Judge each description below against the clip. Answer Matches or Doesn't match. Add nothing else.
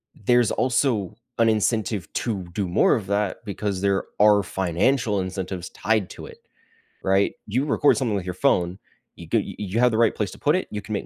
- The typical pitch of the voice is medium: Doesn't match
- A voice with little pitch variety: Doesn't match